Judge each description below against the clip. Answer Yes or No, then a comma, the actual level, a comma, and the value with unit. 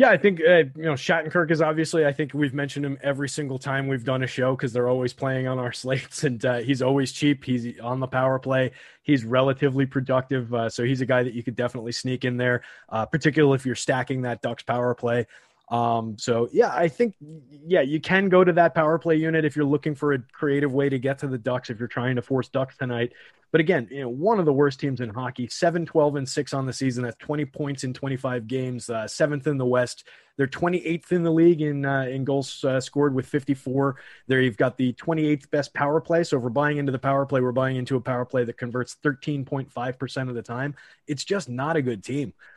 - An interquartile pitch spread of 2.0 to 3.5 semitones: Yes, average, 2.9 semitones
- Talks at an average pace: No, fast, 250 wpm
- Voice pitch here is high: No, low, 135 Hz